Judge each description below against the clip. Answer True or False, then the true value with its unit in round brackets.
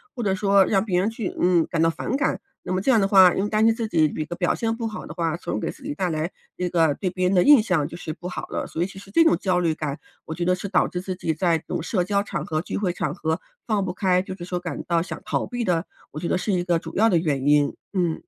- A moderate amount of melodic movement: True (3.2 semitones)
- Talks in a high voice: False (180 Hz)